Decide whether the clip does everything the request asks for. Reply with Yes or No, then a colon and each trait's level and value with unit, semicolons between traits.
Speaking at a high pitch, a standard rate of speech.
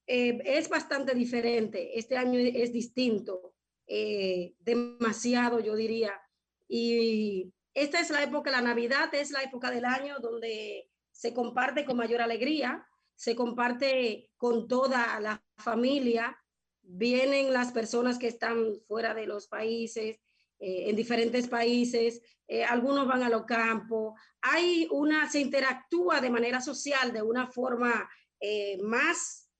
Yes: high, 240 Hz; average, 135 wpm